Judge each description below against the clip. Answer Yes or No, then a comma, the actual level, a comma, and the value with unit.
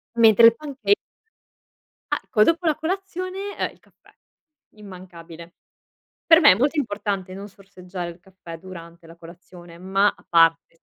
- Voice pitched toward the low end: No, high, 195 Hz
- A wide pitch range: Yes, wide, 8.2 semitones